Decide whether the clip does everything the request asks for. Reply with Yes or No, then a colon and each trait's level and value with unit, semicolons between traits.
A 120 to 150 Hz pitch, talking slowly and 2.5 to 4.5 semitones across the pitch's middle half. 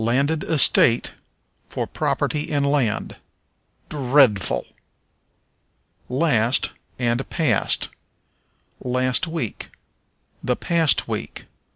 Yes: low, 135 Hz; slow, 75 wpm; average, 3.6 semitones